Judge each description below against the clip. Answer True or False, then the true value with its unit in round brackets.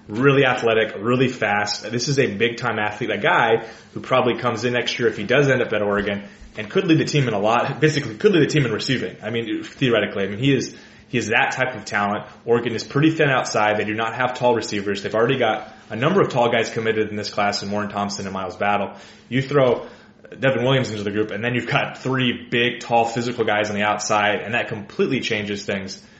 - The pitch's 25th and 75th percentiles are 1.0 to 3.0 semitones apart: False (3.6 semitones)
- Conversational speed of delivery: False (245 wpm)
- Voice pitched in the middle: False (115 Hz)